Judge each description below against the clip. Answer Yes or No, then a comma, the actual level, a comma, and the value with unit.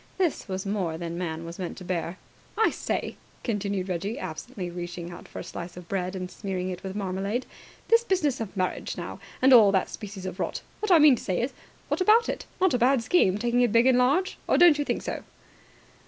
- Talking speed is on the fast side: Yes, fast, 225 wpm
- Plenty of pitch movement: Yes, wide, 6.0 semitones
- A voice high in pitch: Yes, high, 200 Hz